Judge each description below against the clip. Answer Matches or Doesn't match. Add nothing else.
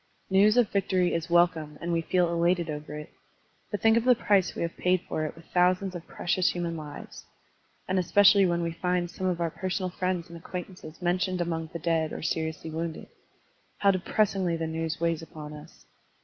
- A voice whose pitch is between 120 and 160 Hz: Doesn't match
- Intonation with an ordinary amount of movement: Doesn't match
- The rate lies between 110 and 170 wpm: Doesn't match